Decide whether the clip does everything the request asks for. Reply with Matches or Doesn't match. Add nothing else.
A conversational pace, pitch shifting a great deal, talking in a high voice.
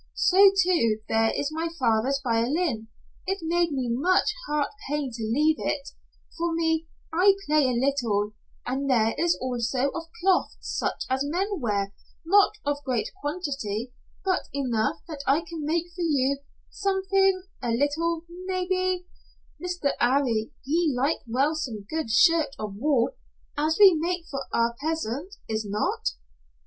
Matches